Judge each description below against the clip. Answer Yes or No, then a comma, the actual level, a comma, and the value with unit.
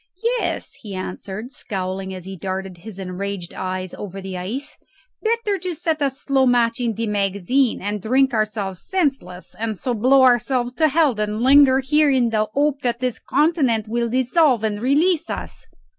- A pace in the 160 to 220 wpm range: Yes, average, 170 wpm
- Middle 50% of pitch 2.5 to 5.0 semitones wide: No, wide, 5.5 semitones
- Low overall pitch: No, high, 235 Hz